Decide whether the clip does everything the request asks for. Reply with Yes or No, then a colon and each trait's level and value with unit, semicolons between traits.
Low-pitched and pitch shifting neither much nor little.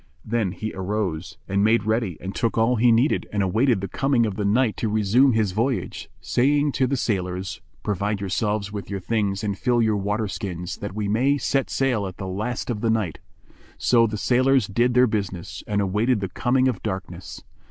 Yes: low, 105 Hz; average, 3.6 semitones